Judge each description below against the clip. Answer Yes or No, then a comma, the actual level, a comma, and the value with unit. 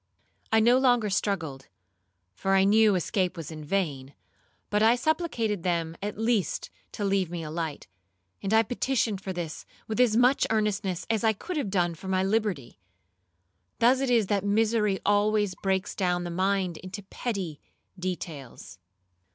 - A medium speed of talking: Yes, average, 160 wpm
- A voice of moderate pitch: No, high, 195 Hz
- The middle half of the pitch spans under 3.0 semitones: No, average, 3.8 semitones